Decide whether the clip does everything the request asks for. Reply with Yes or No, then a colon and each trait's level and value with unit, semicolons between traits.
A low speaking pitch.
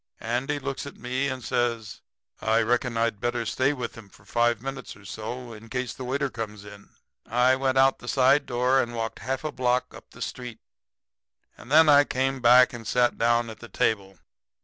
Yes: low, 125 Hz